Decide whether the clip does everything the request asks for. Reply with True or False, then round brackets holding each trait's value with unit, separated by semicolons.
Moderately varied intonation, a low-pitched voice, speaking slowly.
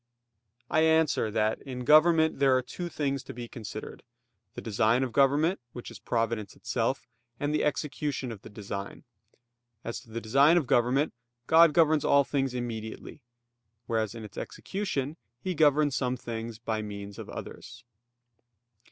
False (4.9 semitones; 130 Hz; 155 wpm)